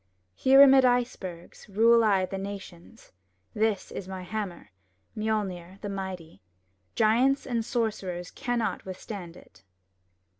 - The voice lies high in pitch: Yes, high, 205 Hz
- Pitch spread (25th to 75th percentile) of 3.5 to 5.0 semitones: Yes, average, 3.8 semitones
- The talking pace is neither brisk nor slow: No, slow, 115 wpm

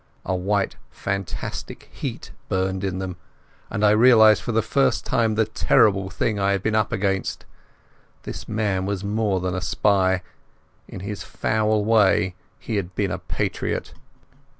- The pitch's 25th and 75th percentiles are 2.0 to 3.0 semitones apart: Yes, narrow, 2.4 semitones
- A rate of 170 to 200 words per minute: No, average, 155 wpm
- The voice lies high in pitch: No, low, 100 Hz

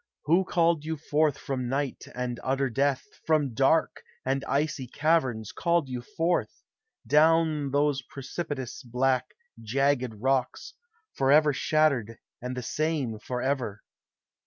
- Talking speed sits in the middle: No, slow, 120 wpm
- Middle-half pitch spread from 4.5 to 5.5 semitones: No, average, 3.4 semitones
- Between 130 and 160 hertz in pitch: Yes, low, 135 Hz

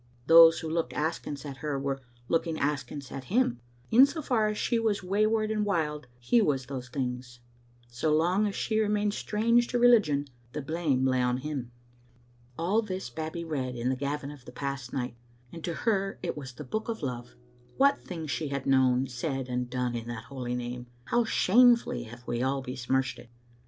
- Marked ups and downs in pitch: Yes, wide, 7.6 semitones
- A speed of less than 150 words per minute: No, average, 200 wpm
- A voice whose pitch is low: No, medium, 145 Hz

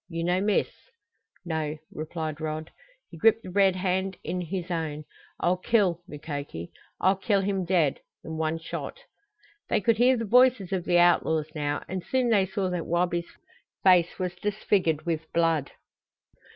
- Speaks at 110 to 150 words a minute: No, average, 160 wpm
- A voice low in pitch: No, medium, 175 Hz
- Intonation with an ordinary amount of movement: Yes, average, 3.4 semitones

